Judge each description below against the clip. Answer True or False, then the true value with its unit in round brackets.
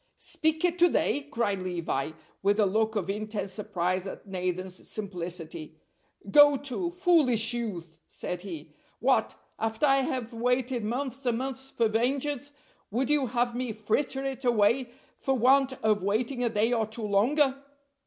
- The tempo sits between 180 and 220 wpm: False (155 wpm)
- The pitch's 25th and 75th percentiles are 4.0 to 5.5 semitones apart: True (5.0 semitones)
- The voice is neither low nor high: False (230 Hz)